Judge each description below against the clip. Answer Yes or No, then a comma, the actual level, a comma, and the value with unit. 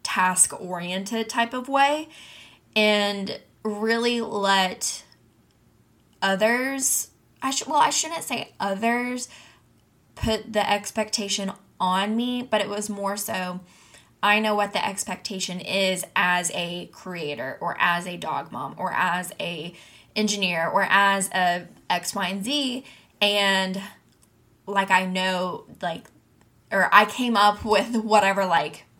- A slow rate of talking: Yes, slow, 130 wpm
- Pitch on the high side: Yes, high, 200 Hz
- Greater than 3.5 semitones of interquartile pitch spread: No, average, 2.9 semitones